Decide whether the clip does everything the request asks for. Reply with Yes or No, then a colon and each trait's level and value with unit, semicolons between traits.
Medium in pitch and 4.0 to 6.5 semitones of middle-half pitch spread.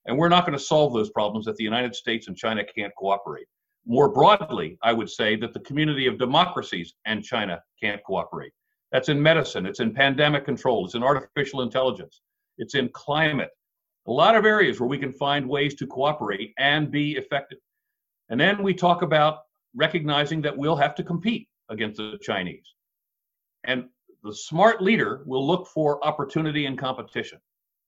Yes: medium, 145 Hz; wide, 5.4 semitones